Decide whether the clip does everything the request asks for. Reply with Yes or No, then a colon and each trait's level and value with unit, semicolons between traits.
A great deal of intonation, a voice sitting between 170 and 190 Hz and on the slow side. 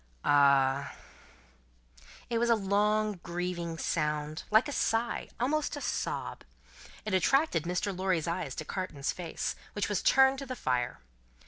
No: wide, 6.5 semitones; medium, 185 Hz; average, 145 wpm